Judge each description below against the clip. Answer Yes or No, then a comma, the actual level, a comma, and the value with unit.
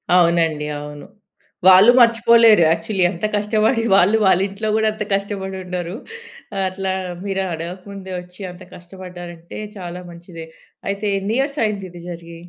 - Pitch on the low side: No, high, 190 Hz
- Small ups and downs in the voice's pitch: No, average, 3.3 semitones